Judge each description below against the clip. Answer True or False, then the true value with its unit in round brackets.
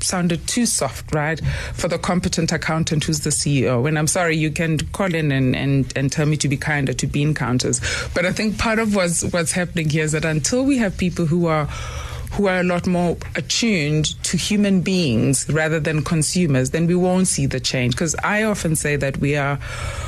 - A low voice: False (160 Hz)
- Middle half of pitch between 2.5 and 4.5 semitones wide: True (3.9 semitones)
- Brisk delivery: True (210 wpm)